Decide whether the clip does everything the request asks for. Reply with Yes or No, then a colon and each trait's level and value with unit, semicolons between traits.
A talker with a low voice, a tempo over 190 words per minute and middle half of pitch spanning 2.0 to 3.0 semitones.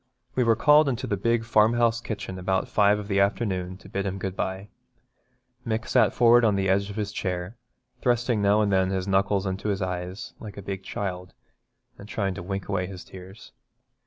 Yes: low, 100 Hz; average, 200 wpm; average, 2.7 semitones